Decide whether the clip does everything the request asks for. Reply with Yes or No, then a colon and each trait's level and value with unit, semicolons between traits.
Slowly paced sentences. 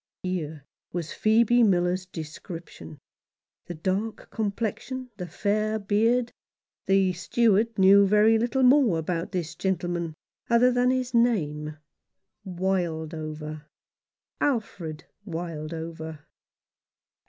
Yes: slow, 95 wpm